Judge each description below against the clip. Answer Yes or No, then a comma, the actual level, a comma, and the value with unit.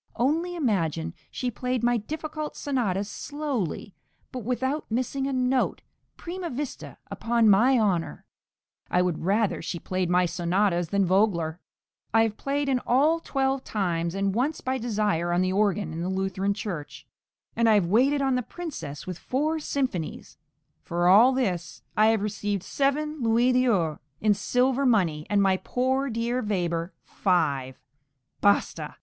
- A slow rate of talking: No, average, 155 wpm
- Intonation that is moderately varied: No, wide, 6.1 semitones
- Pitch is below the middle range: No, high, 215 Hz